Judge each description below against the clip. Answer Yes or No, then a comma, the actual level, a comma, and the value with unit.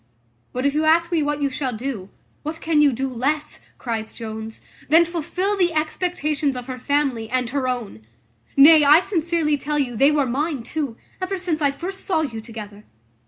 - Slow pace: No, average, 190 wpm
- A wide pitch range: No, average, 4.2 semitones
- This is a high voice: Yes, very high, 285 Hz